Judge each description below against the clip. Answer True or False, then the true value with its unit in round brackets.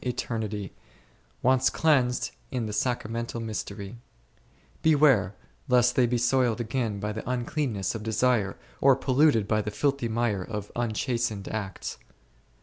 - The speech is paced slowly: True (130 wpm)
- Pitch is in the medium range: False (115 Hz)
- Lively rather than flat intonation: False (3.1 semitones)